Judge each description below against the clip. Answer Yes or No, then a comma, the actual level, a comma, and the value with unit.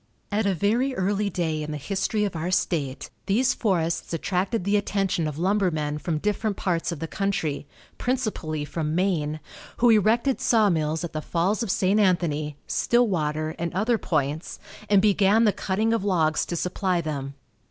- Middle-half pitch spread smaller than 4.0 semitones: No, average, 4.8 semitones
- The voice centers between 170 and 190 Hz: Yes, medium, 185 Hz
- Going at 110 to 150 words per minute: No, average, 165 wpm